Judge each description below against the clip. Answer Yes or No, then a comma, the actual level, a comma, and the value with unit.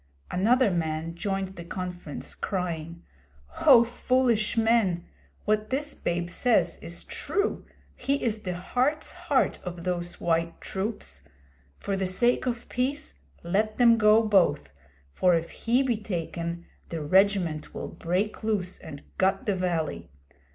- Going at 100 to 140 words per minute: Yes, slow, 135 wpm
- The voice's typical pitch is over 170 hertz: Yes, high, 190 Hz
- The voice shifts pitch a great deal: No, average, 5.0 semitones